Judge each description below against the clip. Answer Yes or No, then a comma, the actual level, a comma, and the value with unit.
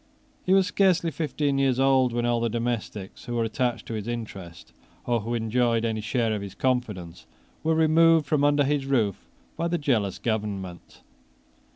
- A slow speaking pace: No, average, 175 wpm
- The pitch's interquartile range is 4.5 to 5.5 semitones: Yes, average, 4.8 semitones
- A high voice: No, low, 120 Hz